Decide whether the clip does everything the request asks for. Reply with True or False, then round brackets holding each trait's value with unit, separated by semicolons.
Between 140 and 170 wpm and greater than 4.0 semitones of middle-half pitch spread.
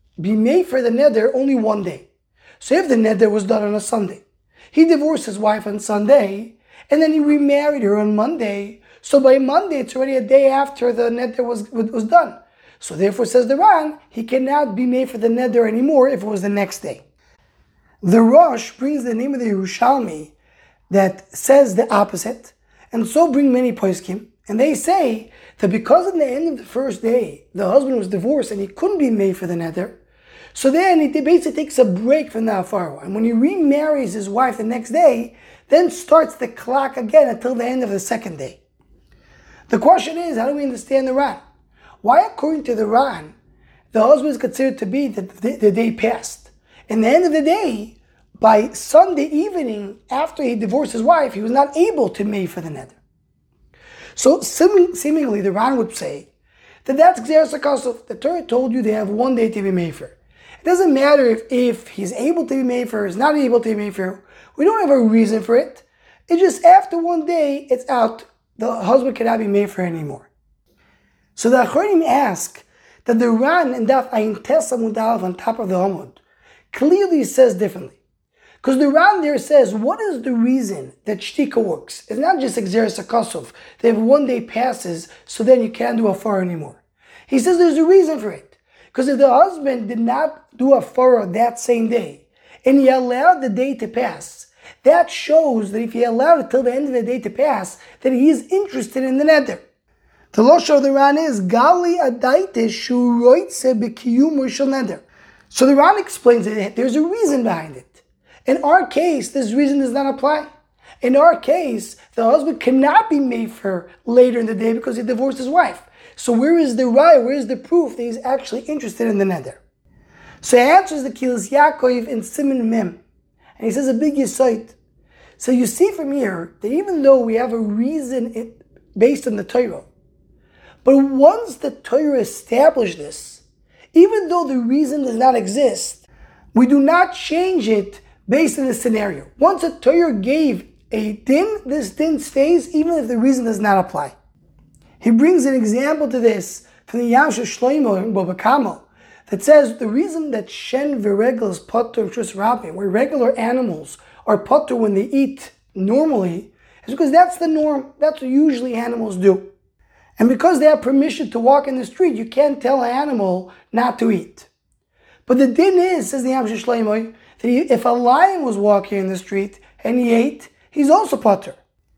False (190 wpm; 4.6 semitones)